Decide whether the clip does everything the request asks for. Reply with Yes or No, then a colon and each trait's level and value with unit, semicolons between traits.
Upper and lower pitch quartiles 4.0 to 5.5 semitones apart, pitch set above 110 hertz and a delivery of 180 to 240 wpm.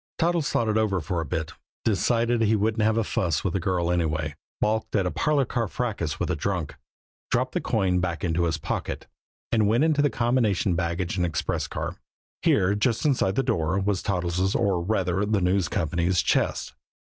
No: average, 4.4 semitones; very low, 95 Hz; average, 195 wpm